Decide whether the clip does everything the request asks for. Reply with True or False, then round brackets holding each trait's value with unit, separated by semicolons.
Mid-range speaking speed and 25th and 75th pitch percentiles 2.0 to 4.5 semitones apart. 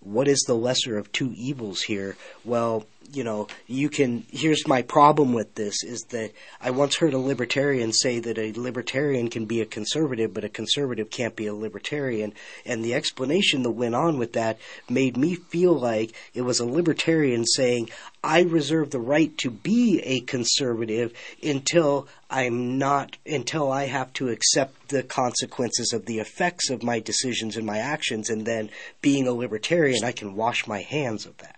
True (180 wpm; 3.9 semitones)